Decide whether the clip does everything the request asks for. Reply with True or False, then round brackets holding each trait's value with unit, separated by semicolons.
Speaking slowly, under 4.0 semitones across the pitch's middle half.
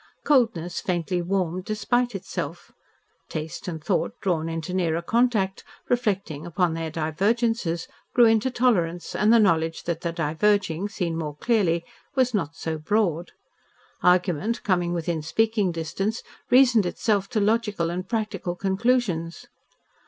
False (130 wpm; 4.8 semitones)